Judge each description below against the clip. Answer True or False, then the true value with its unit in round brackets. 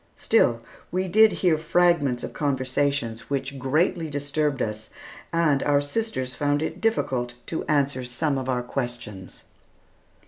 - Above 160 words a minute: False (135 wpm)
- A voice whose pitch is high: False (140 Hz)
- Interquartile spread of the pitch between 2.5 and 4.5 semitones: True (4.0 semitones)